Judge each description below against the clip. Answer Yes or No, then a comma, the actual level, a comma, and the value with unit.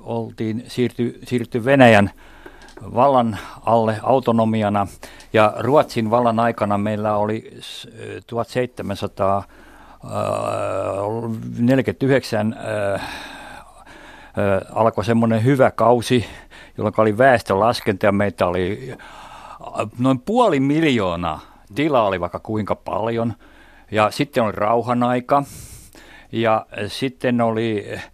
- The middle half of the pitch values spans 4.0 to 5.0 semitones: No, average, 2.7 semitones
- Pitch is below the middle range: Yes, low, 115 Hz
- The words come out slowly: Yes, slow, 85 wpm